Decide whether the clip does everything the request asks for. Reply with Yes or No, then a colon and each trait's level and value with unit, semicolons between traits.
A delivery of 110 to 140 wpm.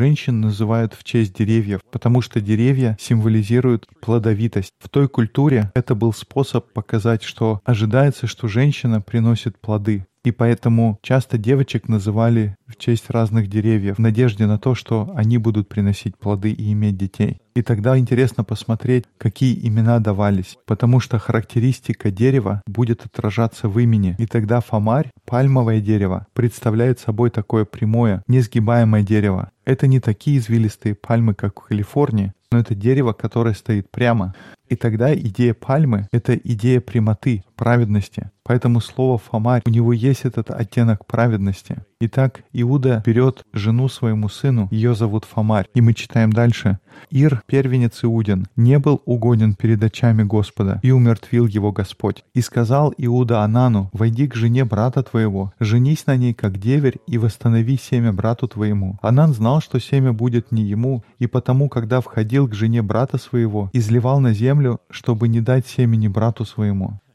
No: average, 150 wpm